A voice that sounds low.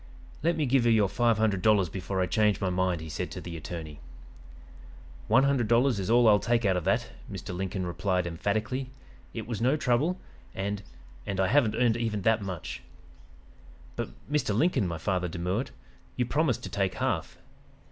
Yes: low, 105 Hz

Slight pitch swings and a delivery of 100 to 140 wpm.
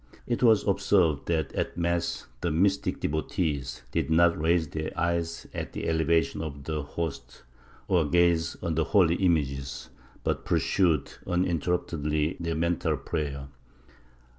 Yes: narrow, 2.1 semitones; slow, 135 wpm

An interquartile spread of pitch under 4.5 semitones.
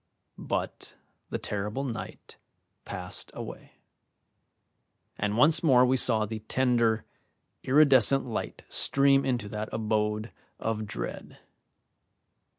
Yes: average, 3.7 semitones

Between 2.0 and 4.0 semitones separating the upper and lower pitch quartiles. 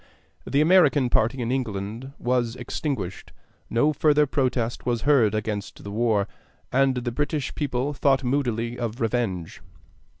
Yes: average, 3.4 semitones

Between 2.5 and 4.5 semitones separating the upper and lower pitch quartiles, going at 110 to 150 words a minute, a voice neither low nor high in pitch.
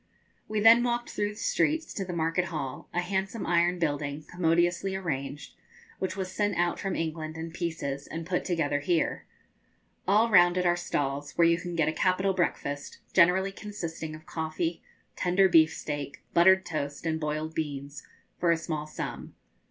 No: average, 3.1 semitones; average, 170 wpm; medium, 170 Hz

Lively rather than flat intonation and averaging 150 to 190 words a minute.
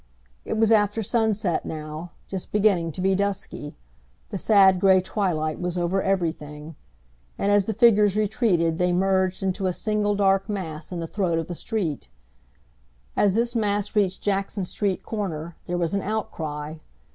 No: average, 3.3 semitones; average, 160 wpm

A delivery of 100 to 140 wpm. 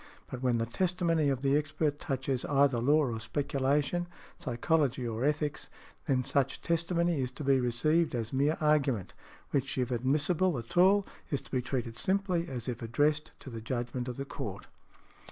No: average, 170 wpm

